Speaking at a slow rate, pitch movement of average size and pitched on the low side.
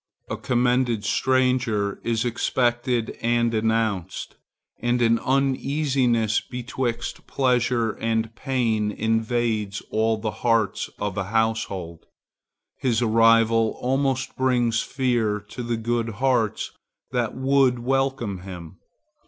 No: slow, 105 wpm; narrow, 2.3 semitones; low, 115 Hz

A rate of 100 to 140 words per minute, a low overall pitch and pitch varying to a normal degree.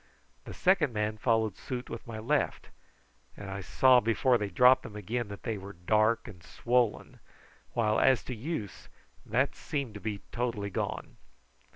No: average, 165 wpm; low, 110 Hz; average, 3.2 semitones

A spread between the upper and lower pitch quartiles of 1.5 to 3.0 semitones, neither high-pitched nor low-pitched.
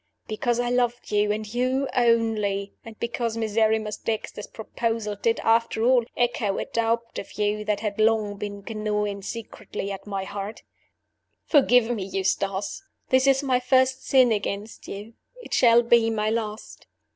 No: narrow, 2.4 semitones; high, 225 Hz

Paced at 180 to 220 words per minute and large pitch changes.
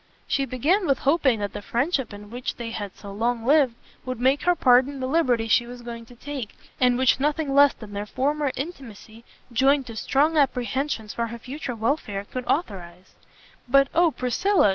No: average, 185 wpm; average, 3.6 semitones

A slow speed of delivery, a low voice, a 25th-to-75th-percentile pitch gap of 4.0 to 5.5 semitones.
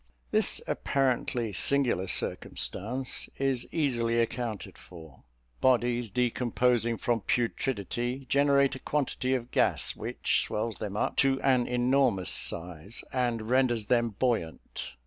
No: slow, 115 wpm; low, 120 Hz; average, 2.9 semitones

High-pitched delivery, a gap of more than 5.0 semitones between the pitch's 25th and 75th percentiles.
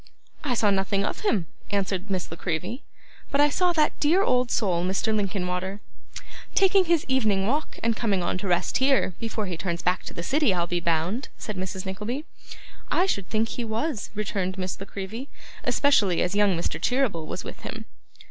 Yes: high, 205 Hz; wide, 5.6 semitones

